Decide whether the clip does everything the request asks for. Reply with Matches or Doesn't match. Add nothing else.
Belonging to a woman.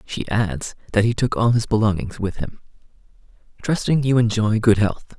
Doesn't match